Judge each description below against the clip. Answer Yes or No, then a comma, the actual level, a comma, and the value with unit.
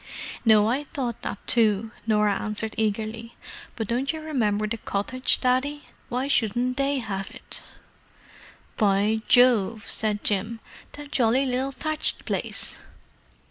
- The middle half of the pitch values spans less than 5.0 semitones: Yes, average, 3.3 semitones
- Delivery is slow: Yes, slow, 130 wpm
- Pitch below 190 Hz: No, high, 230 Hz